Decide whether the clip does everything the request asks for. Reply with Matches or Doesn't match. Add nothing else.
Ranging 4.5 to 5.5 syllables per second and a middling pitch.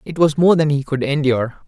Doesn't match